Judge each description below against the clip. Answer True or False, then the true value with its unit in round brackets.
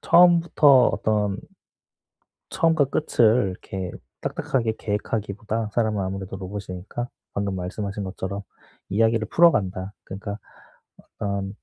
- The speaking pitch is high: False (105 Hz)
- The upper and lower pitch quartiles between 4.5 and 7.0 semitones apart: False (3.0 semitones)